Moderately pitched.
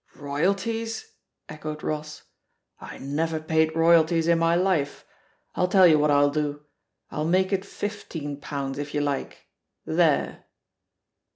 Yes: medium, 160 Hz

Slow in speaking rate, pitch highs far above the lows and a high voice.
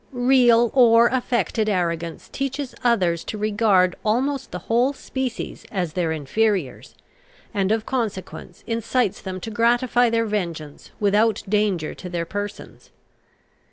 No: slow, 125 wpm; average, 4.5 semitones; high, 215 Hz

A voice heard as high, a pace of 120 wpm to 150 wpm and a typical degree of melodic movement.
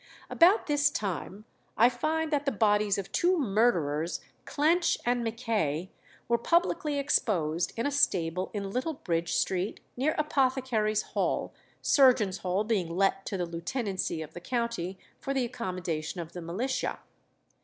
No: high, 215 Hz; average, 145 wpm; wide, 6.8 semitones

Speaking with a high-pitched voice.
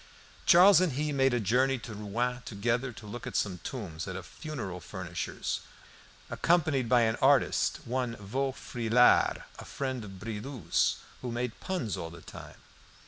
No: low, 120 Hz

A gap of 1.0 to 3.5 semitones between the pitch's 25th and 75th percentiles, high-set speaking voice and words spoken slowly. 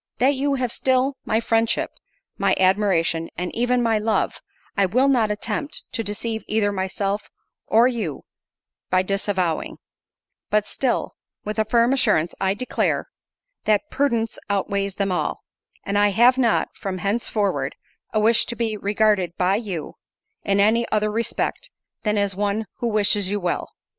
No: average, 2.9 semitones; high, 210 Hz; average, 155 wpm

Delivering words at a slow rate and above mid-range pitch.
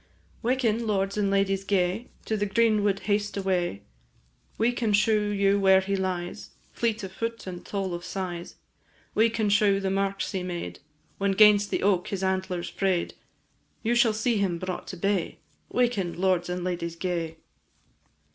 No: average, 165 wpm; high, 195 Hz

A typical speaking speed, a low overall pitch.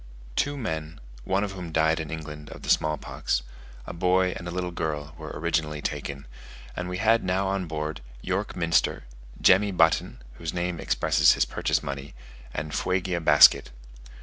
Yes: average, 170 wpm; very low, 85 Hz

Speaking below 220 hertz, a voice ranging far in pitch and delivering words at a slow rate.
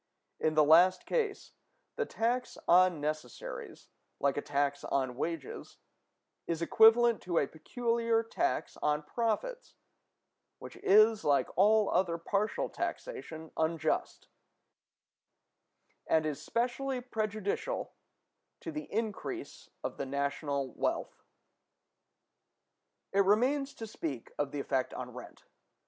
Yes: medium, 185 Hz; wide, 7.6 semitones; slow, 115 wpm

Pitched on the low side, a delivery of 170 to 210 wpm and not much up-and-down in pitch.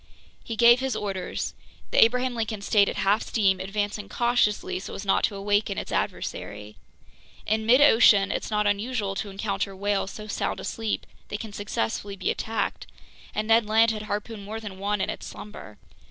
No: high, 210 Hz; average, 175 wpm; narrow, 2.0 semitones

